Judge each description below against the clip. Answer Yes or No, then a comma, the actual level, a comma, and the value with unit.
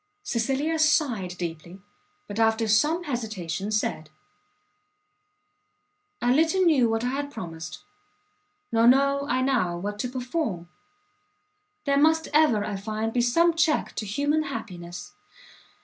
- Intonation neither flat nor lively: No, wide, 5.9 semitones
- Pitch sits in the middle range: No, high, 240 Hz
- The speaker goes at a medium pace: No, slow, 125 wpm